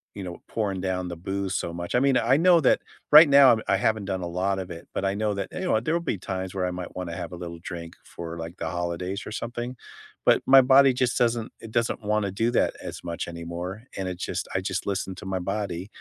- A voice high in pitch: No, very low, 95 Hz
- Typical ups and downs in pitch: Yes, average, 4.7 semitones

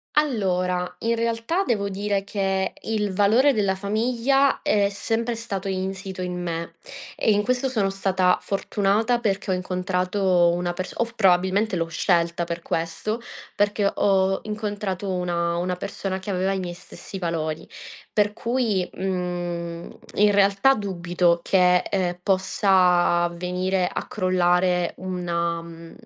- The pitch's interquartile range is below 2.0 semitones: No, narrow, 2.6 semitones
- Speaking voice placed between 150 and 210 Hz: Yes, high, 190 Hz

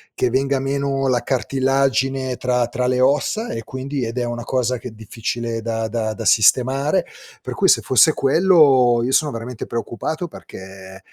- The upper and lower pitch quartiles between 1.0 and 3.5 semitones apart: Yes, average, 2.8 semitones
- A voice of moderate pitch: No, low, 125 Hz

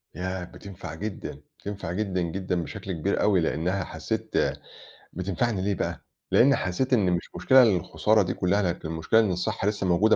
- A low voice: Yes, very low, 95 Hz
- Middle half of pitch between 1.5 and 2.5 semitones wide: No, average, 2.9 semitones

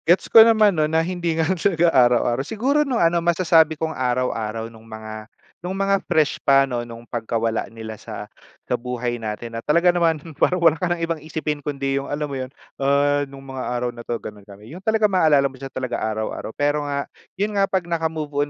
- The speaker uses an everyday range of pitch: No, wide, 5.9 semitones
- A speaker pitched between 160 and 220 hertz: No, medium, 145 Hz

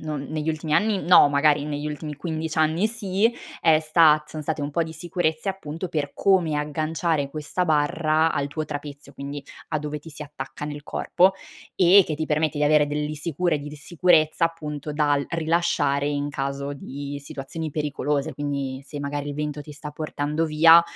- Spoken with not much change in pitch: Yes, narrow, 1.8 semitones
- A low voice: No, medium, 150 Hz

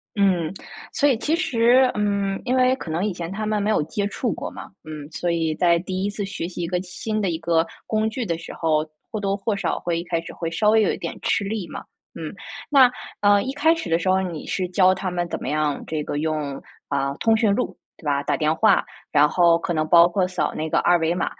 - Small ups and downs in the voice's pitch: No, average, 4.3 semitones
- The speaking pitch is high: No, medium, 180 Hz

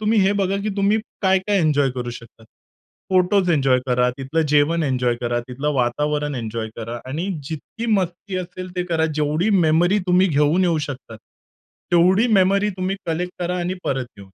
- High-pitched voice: No, medium, 165 Hz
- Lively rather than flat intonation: Yes, wide, 5.8 semitones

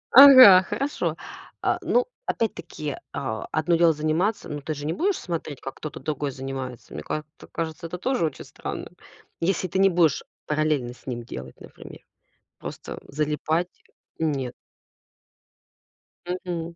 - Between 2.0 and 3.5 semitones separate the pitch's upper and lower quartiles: No, average, 4.1 semitones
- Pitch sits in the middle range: Yes, medium, 155 Hz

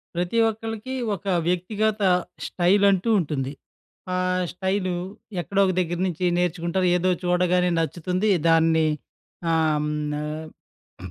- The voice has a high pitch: No, medium, 180 Hz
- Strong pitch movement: No, narrow, 2.5 semitones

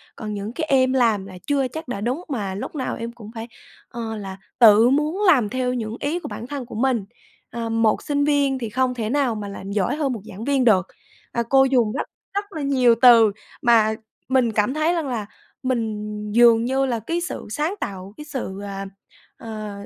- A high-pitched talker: Yes, high, 240 Hz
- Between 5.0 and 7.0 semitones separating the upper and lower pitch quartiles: No, average, 4.0 semitones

